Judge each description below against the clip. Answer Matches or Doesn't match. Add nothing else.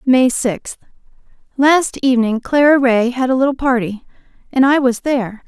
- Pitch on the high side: Matches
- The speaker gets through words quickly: Doesn't match